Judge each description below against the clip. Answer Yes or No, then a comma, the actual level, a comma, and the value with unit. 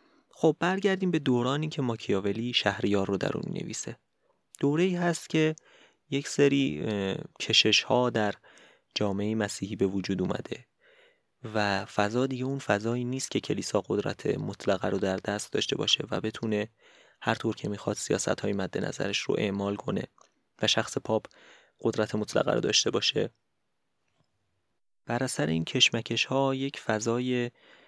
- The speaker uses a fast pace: No, average, 140 wpm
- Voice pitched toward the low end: Yes, low, 115 Hz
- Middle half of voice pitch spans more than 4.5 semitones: Yes, average, 5.2 semitones